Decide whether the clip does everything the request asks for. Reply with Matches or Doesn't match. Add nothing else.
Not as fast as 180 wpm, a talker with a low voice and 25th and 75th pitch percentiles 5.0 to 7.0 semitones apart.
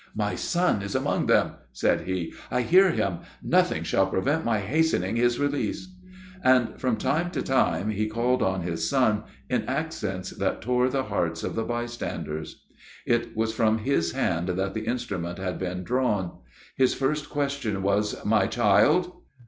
Matches